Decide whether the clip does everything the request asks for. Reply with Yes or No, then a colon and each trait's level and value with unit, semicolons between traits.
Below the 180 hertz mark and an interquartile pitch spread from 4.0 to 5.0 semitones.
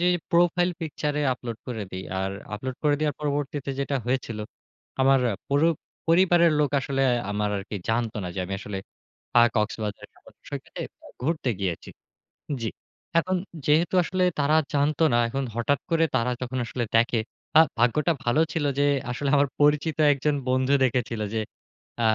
Yes: low, 135 Hz; average, 4.5 semitones